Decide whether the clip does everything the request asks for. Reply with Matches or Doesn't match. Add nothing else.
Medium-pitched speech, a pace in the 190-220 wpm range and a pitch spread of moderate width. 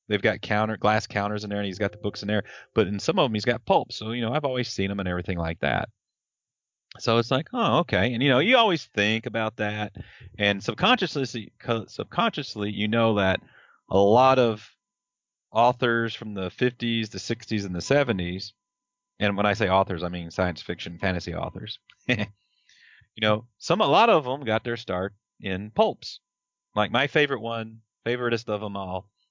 Doesn't match